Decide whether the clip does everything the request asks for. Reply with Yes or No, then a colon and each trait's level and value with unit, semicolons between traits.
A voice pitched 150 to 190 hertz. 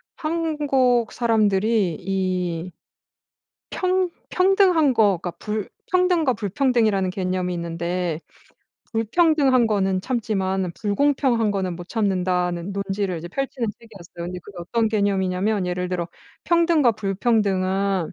No: high, 200 Hz